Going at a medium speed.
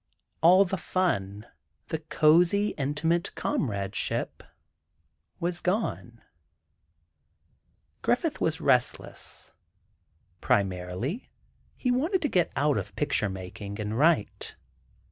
No: slow, 90 wpm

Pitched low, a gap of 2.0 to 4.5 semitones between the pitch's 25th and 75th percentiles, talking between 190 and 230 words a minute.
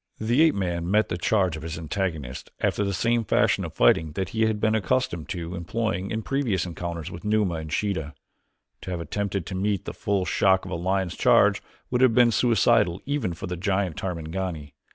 Yes: very low, 95 Hz; average, 4.2 semitones; average, 200 wpm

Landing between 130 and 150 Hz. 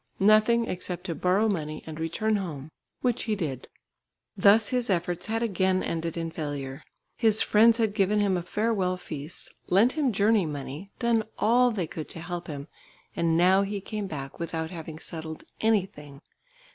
No: medium, 185 Hz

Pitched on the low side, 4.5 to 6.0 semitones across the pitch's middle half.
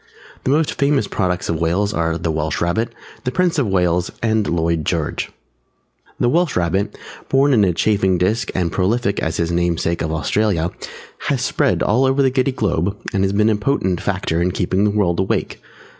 Yes: very low, 95 Hz; average, 5.1 semitones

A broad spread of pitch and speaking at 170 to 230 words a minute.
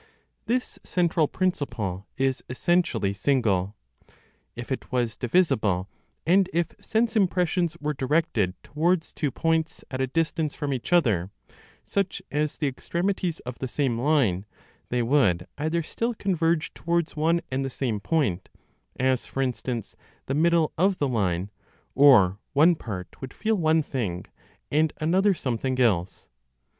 No: wide, 6.2 semitones; average, 140 wpm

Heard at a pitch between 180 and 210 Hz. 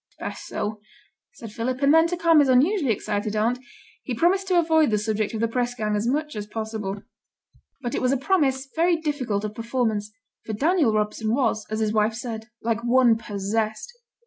No: high, 230 Hz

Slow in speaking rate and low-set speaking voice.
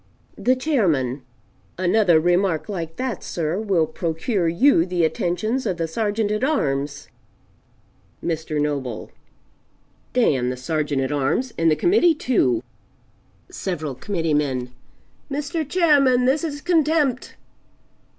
No: slow, 120 wpm; medium, 175 Hz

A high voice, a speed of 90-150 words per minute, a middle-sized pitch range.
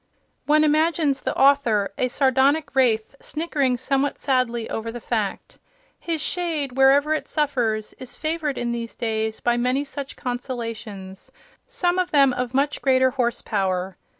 Yes: very high, 260 Hz; average, 145 wpm; average, 3.8 semitones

